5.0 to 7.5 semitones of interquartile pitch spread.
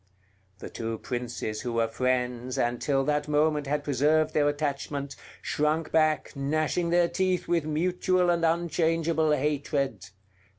No: average, 3.3 semitones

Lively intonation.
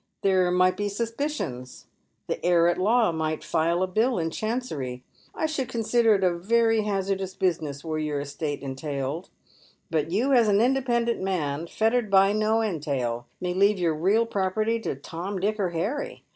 Yes: wide, 5.8 semitones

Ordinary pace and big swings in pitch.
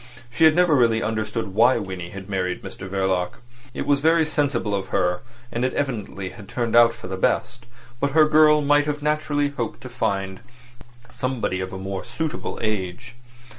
Yes: average, 175 wpm; wide, 7.0 semitones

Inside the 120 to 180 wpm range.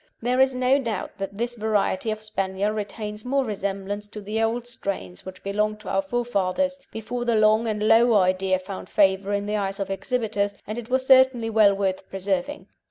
No: average, 190 wpm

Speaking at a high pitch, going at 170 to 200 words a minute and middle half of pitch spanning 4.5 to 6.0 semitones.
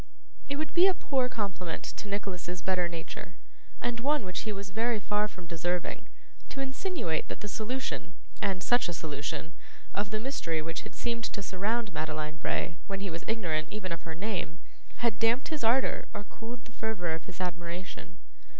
Yes: high, 195 Hz; average, 185 wpm; average, 5.1 semitones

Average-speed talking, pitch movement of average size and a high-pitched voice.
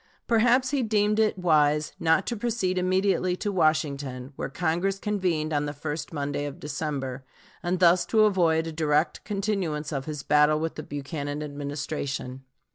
No: average, 160 wpm; average, 4.5 semitones; medium, 160 Hz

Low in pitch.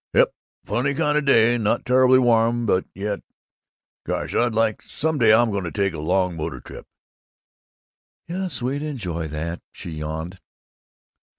Yes: low, 110 Hz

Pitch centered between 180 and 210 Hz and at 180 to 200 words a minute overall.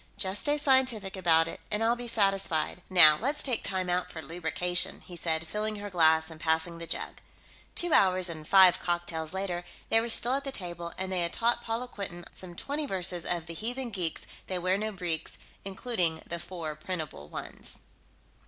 Yes: medium, 185 Hz; average, 190 wpm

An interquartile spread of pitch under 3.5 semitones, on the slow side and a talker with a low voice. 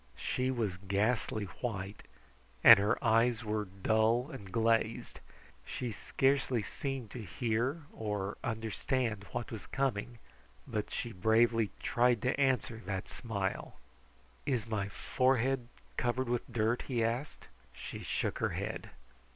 Yes: average, 2.9 semitones; slow, 125 wpm; low, 115 Hz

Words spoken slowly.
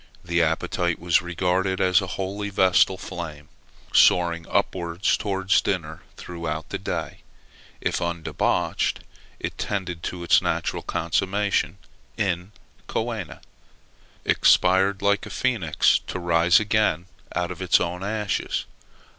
Yes: slow, 120 wpm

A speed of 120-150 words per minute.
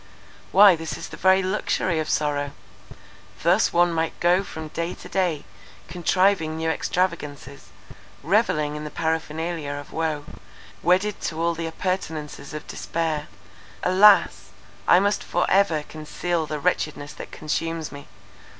Yes: average, 140 wpm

